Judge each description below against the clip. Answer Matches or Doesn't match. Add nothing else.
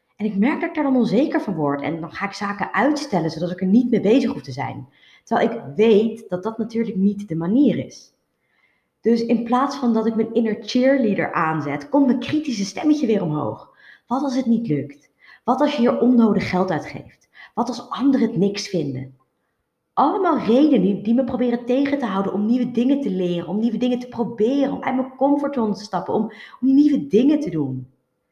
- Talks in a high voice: Matches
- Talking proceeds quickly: Matches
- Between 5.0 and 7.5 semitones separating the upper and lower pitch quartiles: Matches